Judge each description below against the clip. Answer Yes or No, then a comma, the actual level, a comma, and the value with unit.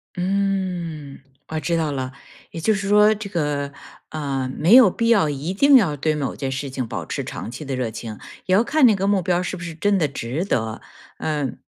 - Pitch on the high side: No, medium, 165 Hz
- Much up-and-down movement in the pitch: Yes, wide, 5.9 semitones